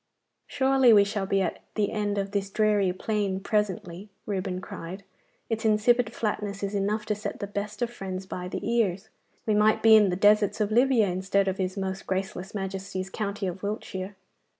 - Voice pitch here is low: No, high, 200 Hz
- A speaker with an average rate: Yes, average, 185 wpm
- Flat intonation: Yes, narrow, 1.9 semitones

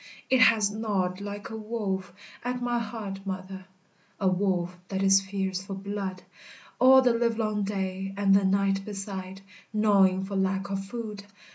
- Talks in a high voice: Yes, high, 195 Hz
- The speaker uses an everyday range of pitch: No, narrow, 1.8 semitones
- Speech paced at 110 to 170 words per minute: Yes, average, 155 wpm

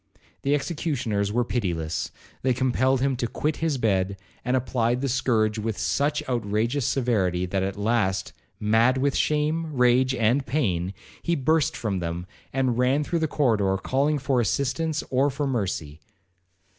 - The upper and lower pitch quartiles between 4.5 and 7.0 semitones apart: Yes, average, 5.1 semitones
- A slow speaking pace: No, average, 155 wpm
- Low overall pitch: Yes, low, 125 Hz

